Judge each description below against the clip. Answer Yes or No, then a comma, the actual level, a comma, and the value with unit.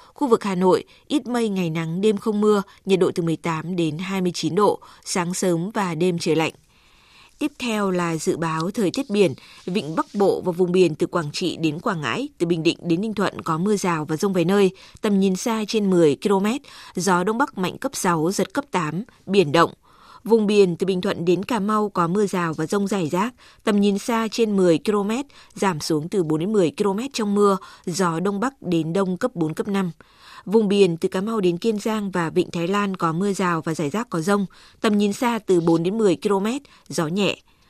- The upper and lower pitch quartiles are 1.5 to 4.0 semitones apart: Yes, average, 3.4 semitones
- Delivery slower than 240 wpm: Yes, average, 230 wpm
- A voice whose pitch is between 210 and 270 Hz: No, high, 190 Hz